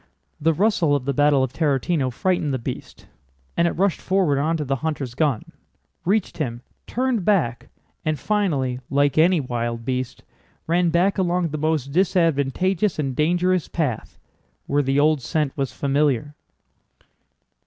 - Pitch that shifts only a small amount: No, average, 4.5 semitones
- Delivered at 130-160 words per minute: Yes, average, 140 wpm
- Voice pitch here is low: No, medium, 150 Hz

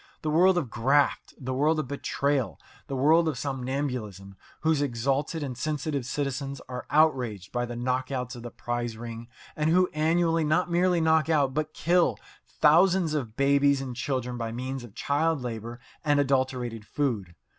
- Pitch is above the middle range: No, medium, 140 Hz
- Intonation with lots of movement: No, average, 4.1 semitones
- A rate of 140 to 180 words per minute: Yes, average, 165 wpm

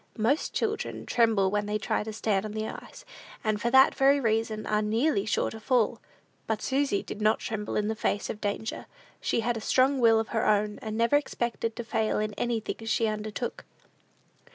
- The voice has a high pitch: Yes, high, 220 Hz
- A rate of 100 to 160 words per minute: No, average, 200 wpm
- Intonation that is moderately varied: No, narrow, 1.9 semitones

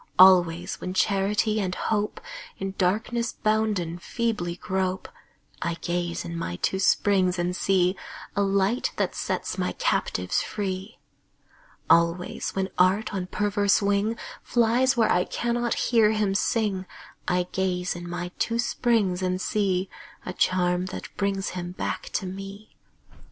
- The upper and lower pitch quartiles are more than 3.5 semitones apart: No, average, 2.8 semitones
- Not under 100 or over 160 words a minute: Yes, average, 140 wpm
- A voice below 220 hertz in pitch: Yes, high, 190 Hz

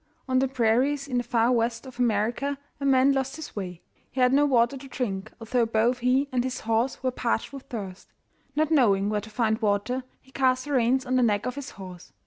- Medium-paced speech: No, fast, 225 wpm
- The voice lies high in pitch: Yes, very high, 250 Hz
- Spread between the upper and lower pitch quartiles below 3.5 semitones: Yes, average, 3.0 semitones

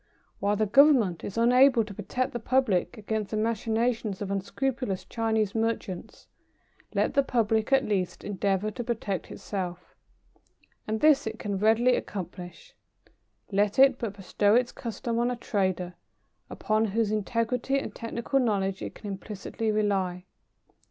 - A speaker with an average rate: Yes, average, 145 wpm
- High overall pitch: Yes, high, 220 Hz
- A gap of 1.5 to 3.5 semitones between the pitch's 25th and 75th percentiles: Yes, average, 3.2 semitones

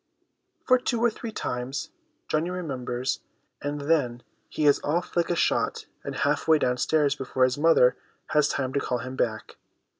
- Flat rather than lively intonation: No, average, 4.4 semitones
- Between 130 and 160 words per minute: No, average, 170 wpm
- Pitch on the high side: No, medium, 145 Hz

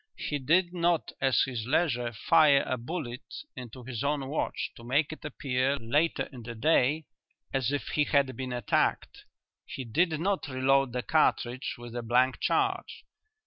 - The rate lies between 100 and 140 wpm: No, average, 165 wpm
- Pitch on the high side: No, low, 135 Hz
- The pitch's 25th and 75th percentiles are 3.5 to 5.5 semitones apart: Yes, average, 4.0 semitones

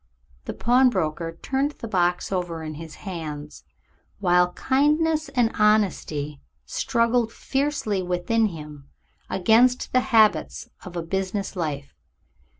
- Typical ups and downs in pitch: No, wide, 6.6 semitones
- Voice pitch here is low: No, high, 190 Hz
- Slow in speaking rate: Yes, slow, 115 wpm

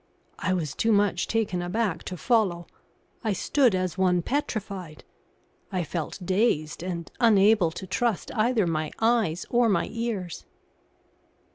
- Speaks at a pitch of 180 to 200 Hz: Yes, high, 190 Hz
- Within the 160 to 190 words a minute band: No, slow, 135 wpm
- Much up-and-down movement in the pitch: No, average, 4.3 semitones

